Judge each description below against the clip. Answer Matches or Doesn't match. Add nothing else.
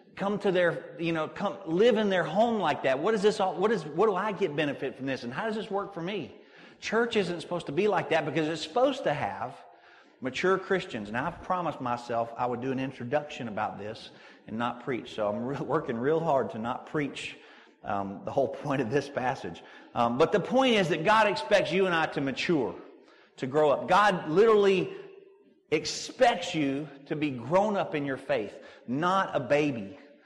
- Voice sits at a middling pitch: Matches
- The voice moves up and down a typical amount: Doesn't match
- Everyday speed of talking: Doesn't match